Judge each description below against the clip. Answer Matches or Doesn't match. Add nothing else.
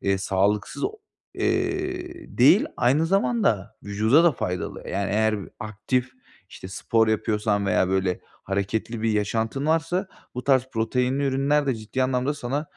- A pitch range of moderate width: Doesn't match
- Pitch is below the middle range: Matches